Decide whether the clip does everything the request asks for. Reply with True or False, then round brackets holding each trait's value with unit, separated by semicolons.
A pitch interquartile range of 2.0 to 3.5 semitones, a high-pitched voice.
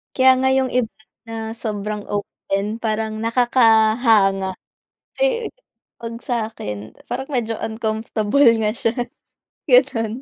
True (2.5 semitones; 225 Hz)